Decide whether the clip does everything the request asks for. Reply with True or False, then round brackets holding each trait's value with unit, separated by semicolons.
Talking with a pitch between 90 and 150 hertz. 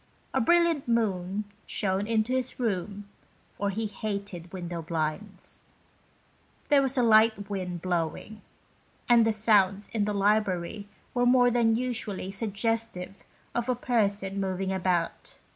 False (205 Hz)